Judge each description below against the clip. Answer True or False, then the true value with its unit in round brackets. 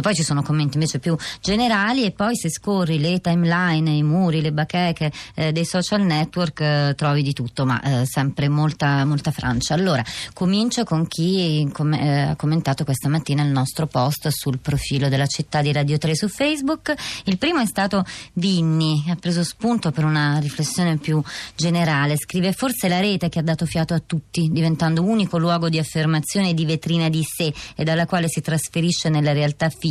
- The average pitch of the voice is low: False (160 Hz)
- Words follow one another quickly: True (185 wpm)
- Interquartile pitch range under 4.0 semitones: True (3.0 semitones)